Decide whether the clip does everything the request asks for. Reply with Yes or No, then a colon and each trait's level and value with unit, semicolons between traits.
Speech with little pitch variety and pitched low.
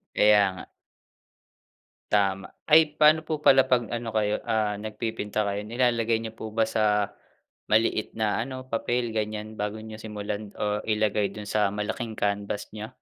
Yes: narrow, 1.8 semitones; low, 110 Hz